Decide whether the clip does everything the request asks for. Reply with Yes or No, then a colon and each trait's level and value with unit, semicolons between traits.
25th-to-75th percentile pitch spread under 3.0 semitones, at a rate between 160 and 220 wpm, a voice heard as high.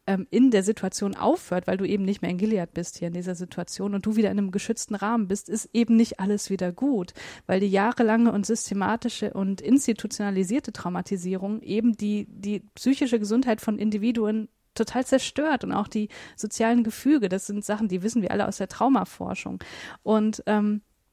Yes: narrow, 2.5 semitones; average, 180 wpm; high, 210 Hz